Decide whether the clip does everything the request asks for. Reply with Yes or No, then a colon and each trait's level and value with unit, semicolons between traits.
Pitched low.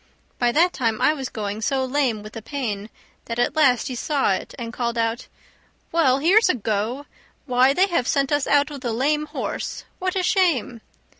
No: very high, 260 Hz